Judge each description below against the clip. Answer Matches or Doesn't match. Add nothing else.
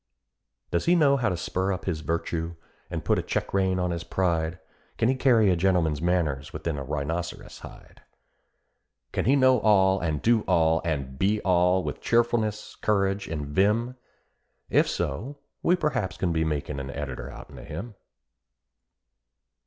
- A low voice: Matches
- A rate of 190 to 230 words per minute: Doesn't match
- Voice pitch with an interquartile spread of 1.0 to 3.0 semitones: Doesn't match